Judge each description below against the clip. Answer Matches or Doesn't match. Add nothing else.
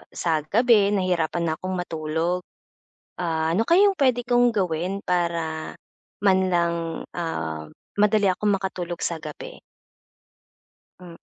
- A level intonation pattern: Doesn't match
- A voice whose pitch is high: Doesn't match